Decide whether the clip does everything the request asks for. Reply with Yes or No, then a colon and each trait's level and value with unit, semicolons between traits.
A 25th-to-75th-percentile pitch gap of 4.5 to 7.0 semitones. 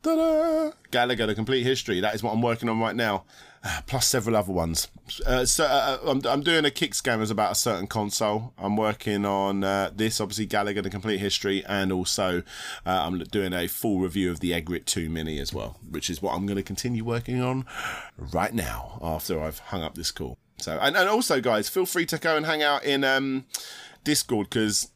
Yes: average, 4.8 semitones